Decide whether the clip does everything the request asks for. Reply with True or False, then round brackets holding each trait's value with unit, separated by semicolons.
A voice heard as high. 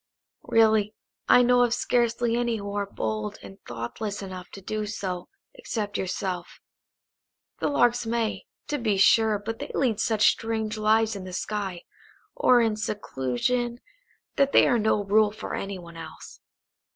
True (215 Hz)